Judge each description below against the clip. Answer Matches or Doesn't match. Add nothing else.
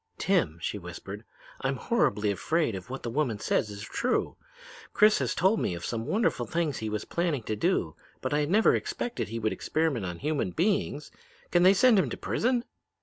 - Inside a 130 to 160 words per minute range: Doesn't match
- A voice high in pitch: Doesn't match